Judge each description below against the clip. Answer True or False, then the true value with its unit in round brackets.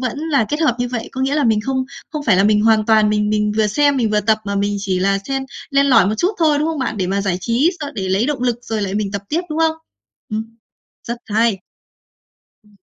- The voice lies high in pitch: True (225 Hz)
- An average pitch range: True (4.9 semitones)